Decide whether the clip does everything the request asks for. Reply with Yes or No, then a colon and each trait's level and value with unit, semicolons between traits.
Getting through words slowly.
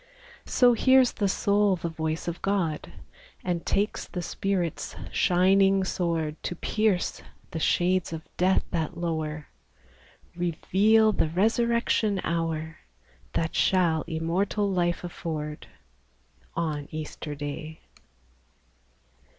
Yes: slow, 110 wpm